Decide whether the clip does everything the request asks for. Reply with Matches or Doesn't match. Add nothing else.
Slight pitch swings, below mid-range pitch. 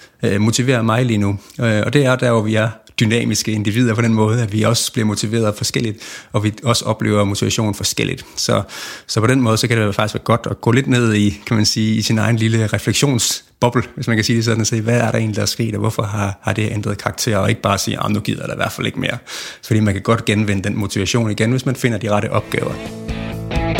Matches